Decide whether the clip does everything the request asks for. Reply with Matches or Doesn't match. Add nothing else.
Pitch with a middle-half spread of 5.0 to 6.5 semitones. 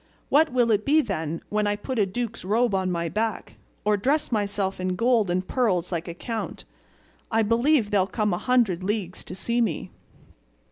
Doesn't match